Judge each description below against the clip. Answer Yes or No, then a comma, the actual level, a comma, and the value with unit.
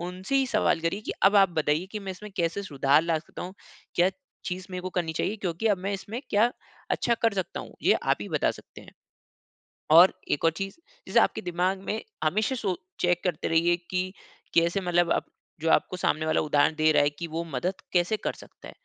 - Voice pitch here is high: No, medium, 180 Hz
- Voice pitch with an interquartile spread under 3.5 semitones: Yes, average, 3.0 semitones